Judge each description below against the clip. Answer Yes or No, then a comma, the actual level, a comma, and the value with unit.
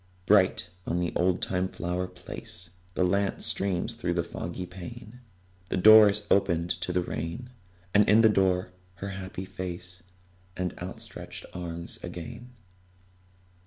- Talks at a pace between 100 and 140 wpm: Yes, slow, 135 wpm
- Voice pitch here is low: Yes, very low, 90 Hz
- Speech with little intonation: Yes, narrow, 2.3 semitones